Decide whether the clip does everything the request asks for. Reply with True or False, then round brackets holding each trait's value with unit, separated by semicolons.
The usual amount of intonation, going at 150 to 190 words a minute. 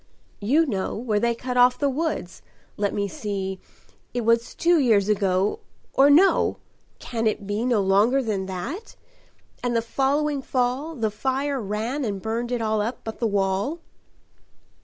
True (4.6 semitones; 160 wpm)